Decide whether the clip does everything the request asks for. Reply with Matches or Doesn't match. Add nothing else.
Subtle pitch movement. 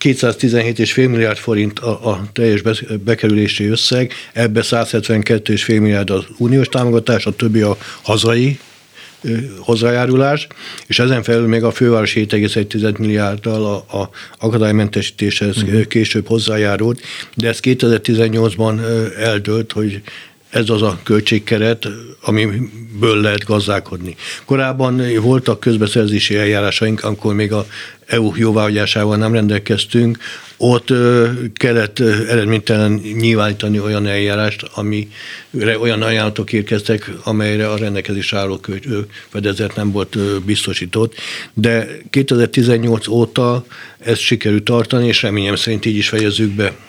Matches